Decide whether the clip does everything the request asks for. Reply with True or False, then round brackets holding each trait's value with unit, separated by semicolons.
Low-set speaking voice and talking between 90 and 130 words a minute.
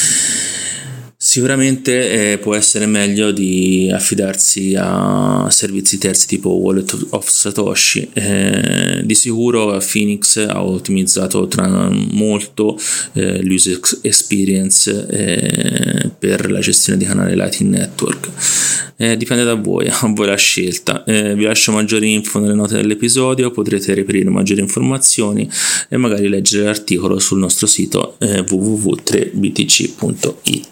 True (105 Hz; 120 wpm)